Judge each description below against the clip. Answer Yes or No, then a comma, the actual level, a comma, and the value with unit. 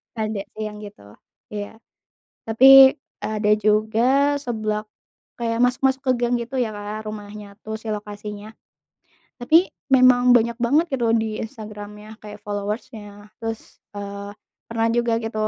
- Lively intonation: No, narrow, 2.4 semitones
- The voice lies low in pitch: No, high, 220 Hz